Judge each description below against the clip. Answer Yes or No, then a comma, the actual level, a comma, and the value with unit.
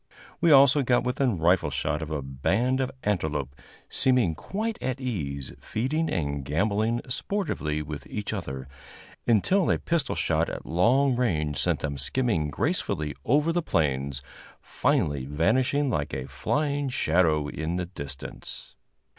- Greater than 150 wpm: No, average, 140 wpm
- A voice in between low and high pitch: No, very low, 90 Hz